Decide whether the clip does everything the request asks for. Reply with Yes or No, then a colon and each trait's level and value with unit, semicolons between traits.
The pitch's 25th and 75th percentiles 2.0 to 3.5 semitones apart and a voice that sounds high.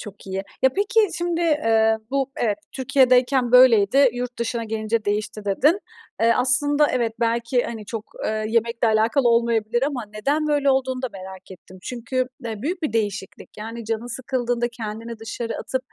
Yes: average, 3.0 semitones; high, 235 Hz